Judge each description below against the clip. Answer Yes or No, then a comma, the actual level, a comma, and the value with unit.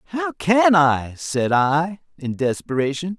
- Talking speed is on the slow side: Yes, slow, 130 wpm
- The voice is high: No, medium, 165 Hz